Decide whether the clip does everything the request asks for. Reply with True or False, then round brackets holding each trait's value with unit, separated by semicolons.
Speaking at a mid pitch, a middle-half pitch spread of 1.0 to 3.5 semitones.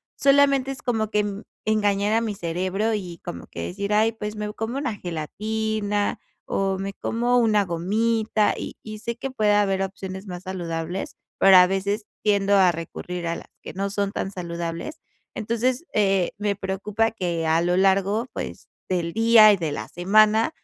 False (205 Hz; 2.9 semitones)